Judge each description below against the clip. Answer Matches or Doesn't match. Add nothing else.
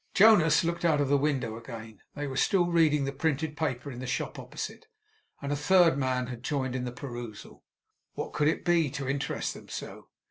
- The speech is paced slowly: Doesn't match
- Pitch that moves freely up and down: Doesn't match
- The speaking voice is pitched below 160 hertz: Matches